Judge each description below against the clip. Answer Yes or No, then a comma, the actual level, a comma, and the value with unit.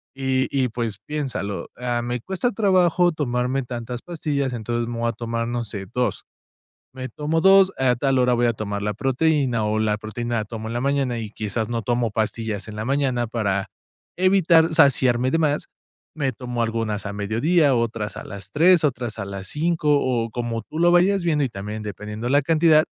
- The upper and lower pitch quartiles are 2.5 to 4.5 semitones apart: No, average, 4.9 semitones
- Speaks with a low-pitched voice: Yes, low, 120 Hz